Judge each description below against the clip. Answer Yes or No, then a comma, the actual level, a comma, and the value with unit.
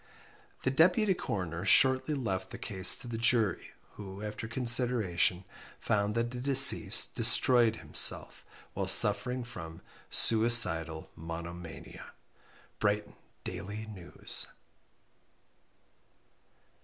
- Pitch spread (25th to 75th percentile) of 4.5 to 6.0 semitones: Yes, average, 4.8 semitones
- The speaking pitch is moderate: No, low, 110 Hz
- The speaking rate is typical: No, slow, 95 wpm